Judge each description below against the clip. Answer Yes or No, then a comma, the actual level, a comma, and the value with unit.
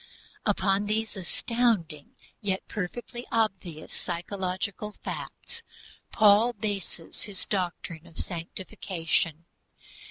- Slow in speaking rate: Yes, slow, 85 wpm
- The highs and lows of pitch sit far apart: No, average, 3.7 semitones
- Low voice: No, high, 195 Hz